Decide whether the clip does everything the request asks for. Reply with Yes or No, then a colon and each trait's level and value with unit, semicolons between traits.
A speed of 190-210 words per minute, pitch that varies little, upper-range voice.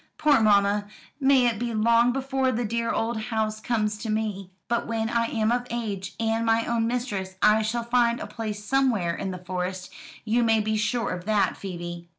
Yes: average, 195 wpm; narrow, 2.3 semitones; high, 225 Hz